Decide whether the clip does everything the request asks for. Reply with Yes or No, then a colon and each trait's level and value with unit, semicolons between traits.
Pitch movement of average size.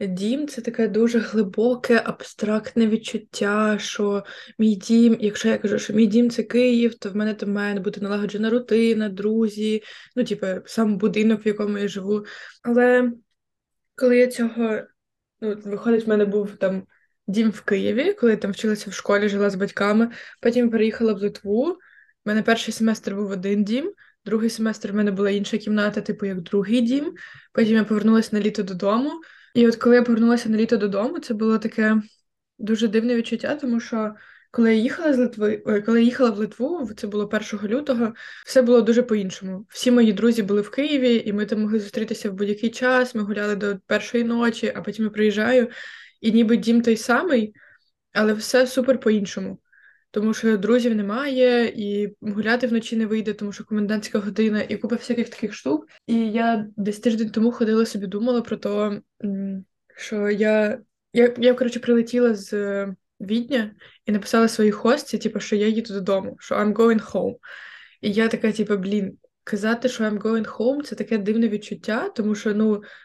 No: narrow, 2.0 semitones